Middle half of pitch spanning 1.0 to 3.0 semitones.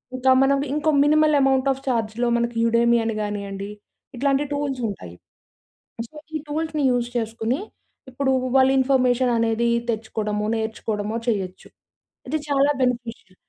No: average, 3.5 semitones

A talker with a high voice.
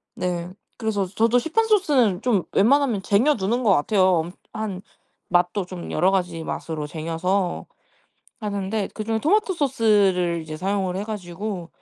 Yes: high, 195 Hz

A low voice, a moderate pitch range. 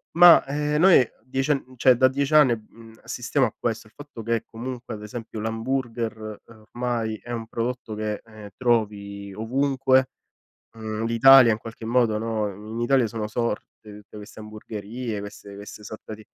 Yes: low, 115 Hz; average, 3.0 semitones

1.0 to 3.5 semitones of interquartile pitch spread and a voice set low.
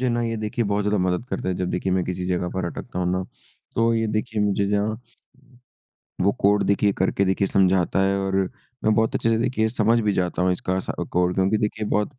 Yes: average, 2.8 semitones; low, 100 Hz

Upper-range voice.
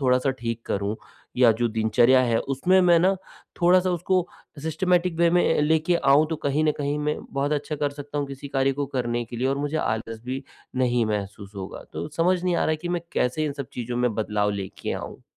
No: medium, 140 Hz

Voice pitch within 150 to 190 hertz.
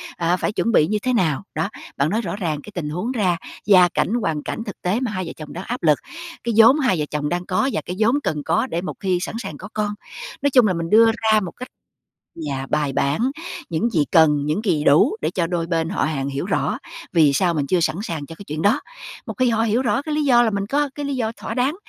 Yes: medium, 185 Hz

